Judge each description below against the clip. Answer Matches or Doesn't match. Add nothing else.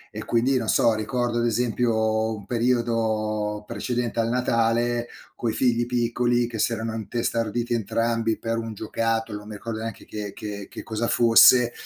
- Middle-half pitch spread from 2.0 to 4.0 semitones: Doesn't match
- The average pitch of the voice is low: Matches